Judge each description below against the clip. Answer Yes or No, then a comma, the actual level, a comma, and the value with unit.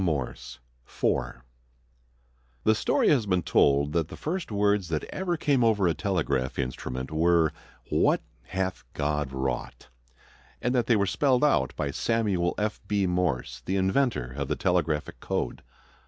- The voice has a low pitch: Yes, very low, 90 Hz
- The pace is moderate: Yes, average, 150 wpm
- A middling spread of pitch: No, wide, 6.7 semitones